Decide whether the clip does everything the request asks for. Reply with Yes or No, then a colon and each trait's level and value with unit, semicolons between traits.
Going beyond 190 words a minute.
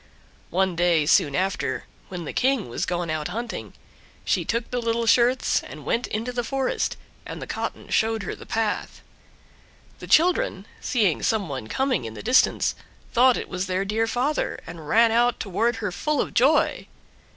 No: average, 175 wpm